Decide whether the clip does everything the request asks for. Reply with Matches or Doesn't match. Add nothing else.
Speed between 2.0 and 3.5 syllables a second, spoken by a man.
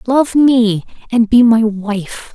Doesn't match